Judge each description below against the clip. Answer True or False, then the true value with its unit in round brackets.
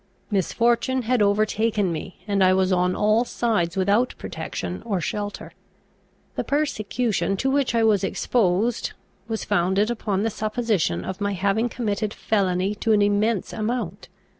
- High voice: True (210 Hz)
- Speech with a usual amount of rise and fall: True (3.1 semitones)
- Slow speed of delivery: False (145 wpm)